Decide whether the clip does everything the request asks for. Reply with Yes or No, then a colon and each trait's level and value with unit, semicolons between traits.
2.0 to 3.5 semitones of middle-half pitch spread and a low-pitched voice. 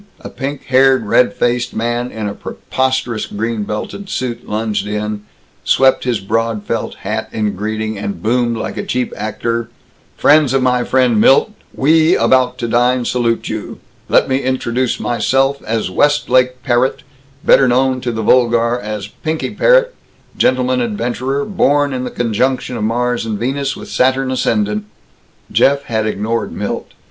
Yes: average, 3.0 semitones; low, 120 Hz